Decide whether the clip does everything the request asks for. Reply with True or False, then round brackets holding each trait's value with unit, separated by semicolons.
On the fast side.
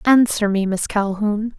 False (150 wpm)